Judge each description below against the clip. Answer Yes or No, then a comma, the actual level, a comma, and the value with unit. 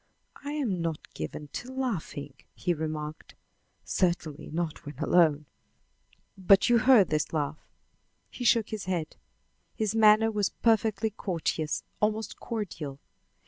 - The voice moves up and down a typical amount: No, wide, 6.1 semitones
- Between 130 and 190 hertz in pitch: Yes, medium, 185 Hz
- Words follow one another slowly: Yes, slow, 125 wpm